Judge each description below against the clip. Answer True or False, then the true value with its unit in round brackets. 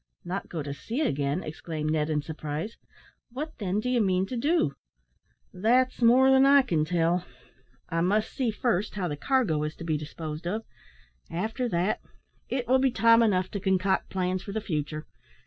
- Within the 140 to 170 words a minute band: False (180 wpm)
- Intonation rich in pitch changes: True (6.5 semitones)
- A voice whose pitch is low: False (190 Hz)